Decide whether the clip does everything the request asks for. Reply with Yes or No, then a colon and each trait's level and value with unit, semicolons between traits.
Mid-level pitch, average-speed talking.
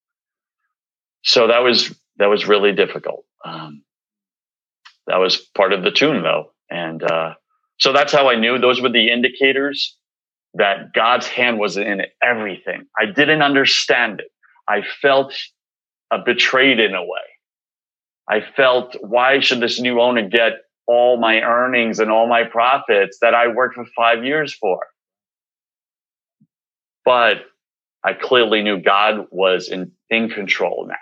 No: low, 120 Hz; average, 145 wpm